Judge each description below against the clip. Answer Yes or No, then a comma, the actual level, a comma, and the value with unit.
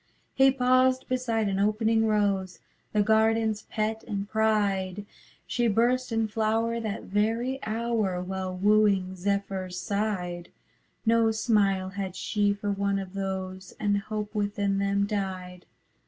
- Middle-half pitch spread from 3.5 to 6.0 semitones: No, narrow, 2.4 semitones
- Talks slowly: Yes, slow, 130 wpm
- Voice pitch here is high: Yes, high, 205 Hz